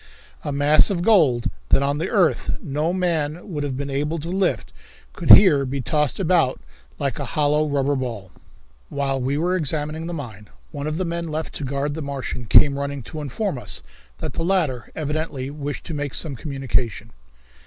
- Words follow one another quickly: No, average, 185 wpm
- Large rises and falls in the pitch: No, average, 2.9 semitones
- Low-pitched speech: No, medium, 145 Hz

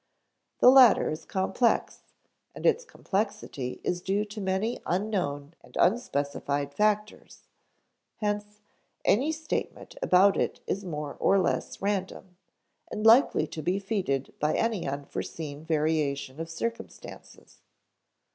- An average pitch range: No, wide, 5.7 semitones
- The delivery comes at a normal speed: No, slow, 120 wpm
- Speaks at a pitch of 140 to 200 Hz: Yes, high, 190 Hz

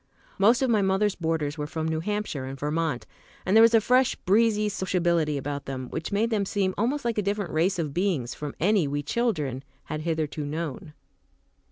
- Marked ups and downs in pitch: Yes, wide, 5.8 semitones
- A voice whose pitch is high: No, medium, 170 Hz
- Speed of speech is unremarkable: Yes, average, 195 wpm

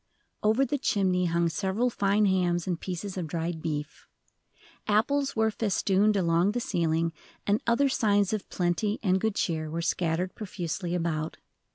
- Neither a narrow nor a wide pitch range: Yes, average, 3.9 semitones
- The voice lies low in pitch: No, medium, 185 Hz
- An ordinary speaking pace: Yes, average, 155 wpm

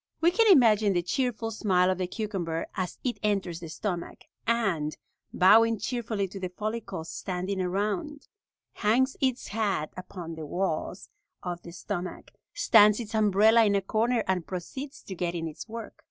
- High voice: Yes, high, 200 Hz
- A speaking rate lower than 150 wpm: No, average, 165 wpm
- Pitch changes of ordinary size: Yes, average, 4.0 semitones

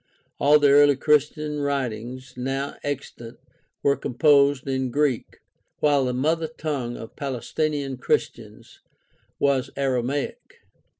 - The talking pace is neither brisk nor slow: No, slow, 110 wpm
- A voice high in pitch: No, medium, 140 Hz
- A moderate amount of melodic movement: No, narrow, 2.3 semitones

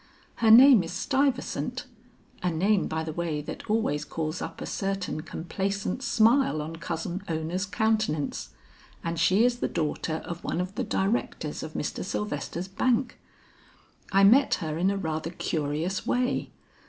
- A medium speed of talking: Yes, average, 155 wpm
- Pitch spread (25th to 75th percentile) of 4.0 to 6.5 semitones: Yes, average, 5.3 semitones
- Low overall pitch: No, medium, 185 Hz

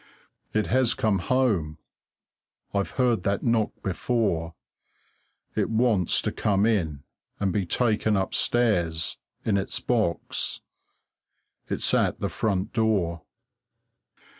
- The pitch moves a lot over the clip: No, average, 4.3 semitones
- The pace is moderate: No, slow, 110 wpm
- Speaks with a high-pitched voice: No, low, 105 Hz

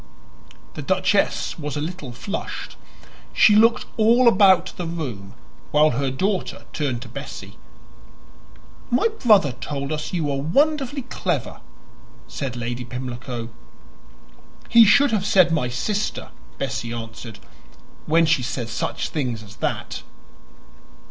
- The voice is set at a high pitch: No, medium, 150 Hz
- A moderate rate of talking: No, slow, 125 wpm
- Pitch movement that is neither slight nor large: No, wide, 8.5 semitones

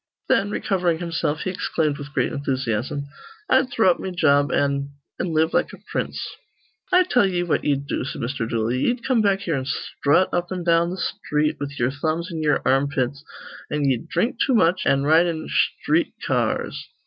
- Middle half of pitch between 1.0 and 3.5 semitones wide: No, average, 4.4 semitones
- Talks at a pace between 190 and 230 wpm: Yes, average, 195 wpm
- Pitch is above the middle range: No, medium, 155 Hz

